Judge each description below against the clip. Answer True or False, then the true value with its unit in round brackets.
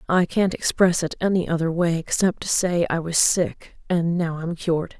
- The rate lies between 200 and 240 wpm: True (205 wpm)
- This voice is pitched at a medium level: True (170 Hz)